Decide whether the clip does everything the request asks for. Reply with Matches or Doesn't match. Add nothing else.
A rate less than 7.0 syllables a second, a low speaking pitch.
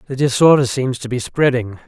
Matches